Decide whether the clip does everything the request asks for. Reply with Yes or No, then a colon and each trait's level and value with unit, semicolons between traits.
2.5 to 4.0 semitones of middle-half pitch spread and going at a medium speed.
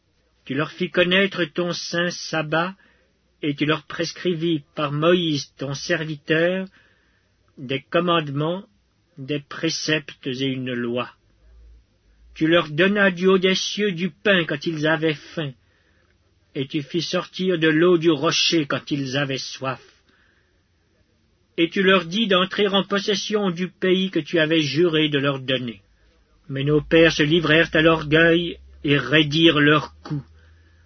No: average, 4.6 semitones; average, 145 wpm